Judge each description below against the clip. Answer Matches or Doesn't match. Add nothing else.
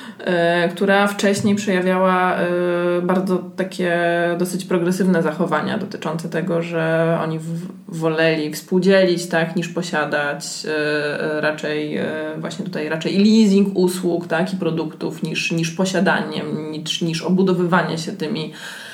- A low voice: Doesn't match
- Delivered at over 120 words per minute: Doesn't match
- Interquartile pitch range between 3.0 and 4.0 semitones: Doesn't match